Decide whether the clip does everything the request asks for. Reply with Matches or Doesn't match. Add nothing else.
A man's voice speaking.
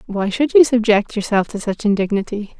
Doesn't match